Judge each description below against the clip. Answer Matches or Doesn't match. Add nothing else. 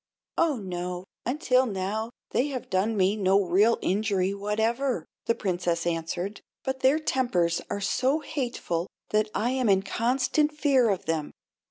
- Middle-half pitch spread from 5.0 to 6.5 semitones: Matches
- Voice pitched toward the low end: Doesn't match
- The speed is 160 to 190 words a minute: Doesn't match